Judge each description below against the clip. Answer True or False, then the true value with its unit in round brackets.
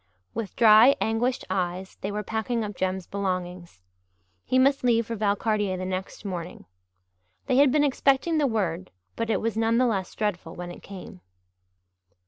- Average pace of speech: True (165 wpm)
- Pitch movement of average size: True (4.0 semitones)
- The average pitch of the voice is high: True (210 Hz)